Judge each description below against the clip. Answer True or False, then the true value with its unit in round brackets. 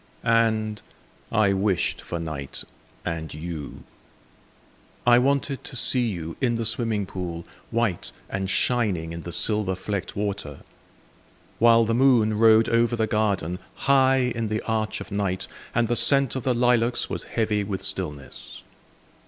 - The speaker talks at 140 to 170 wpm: True (145 wpm)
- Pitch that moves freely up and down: False (4.0 semitones)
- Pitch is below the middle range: True (110 Hz)